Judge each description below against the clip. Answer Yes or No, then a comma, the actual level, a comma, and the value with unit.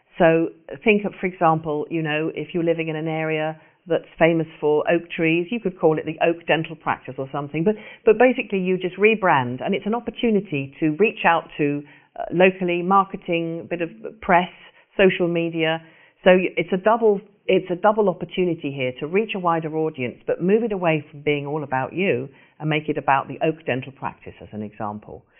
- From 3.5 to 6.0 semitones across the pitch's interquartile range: Yes, average, 3.8 semitones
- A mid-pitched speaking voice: Yes, medium, 165 Hz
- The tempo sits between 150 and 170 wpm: No, average, 200 wpm